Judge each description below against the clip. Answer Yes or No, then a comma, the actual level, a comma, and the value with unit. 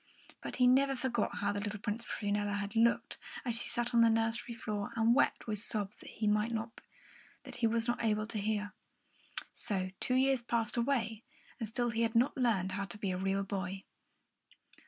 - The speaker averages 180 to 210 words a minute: Yes, average, 185 wpm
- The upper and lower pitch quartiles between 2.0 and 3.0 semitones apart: Yes, narrow, 2.4 semitones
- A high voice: Yes, high, 225 Hz